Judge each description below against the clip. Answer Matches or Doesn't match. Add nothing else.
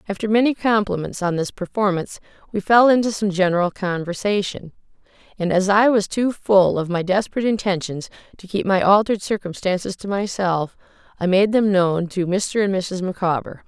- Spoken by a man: Doesn't match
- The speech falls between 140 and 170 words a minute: Matches